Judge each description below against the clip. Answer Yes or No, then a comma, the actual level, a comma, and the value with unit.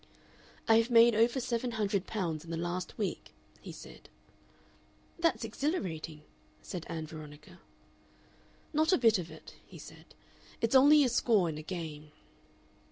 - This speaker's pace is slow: No, average, 150 wpm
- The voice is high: Yes, high, 200 Hz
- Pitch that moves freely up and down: Yes, wide, 6.6 semitones